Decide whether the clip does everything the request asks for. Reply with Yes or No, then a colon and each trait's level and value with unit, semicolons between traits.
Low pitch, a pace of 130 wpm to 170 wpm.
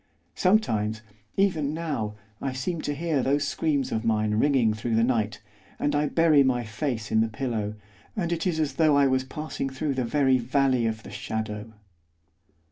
No: low, 130 Hz; average, 180 wpm